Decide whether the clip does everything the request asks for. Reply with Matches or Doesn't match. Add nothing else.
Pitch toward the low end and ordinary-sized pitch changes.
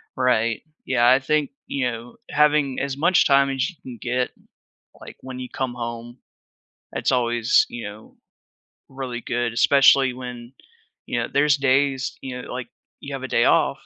Doesn't match